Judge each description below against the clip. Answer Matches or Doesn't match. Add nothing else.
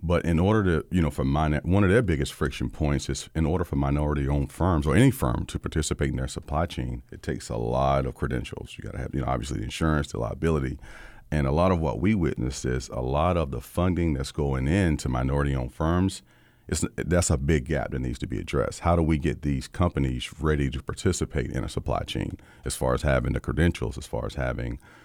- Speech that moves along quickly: Matches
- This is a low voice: Matches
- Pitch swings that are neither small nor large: Matches